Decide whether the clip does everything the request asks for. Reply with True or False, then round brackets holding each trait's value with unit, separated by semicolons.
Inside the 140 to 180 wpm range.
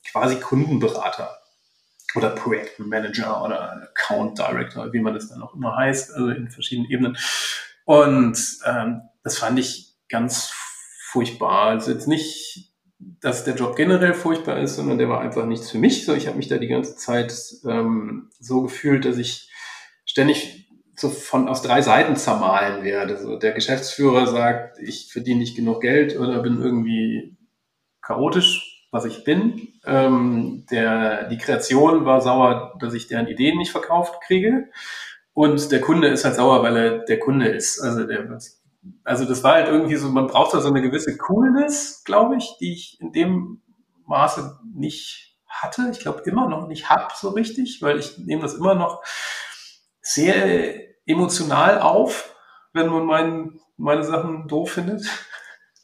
True (160 wpm)